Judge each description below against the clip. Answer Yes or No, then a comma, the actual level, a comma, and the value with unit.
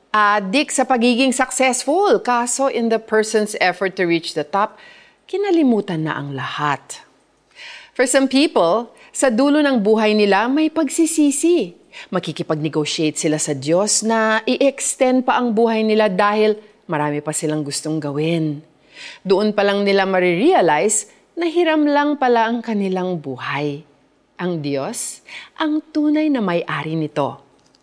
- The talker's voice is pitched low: No, high, 215 Hz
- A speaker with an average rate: Yes, average, 135 wpm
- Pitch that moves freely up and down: Yes, wide, 8.3 semitones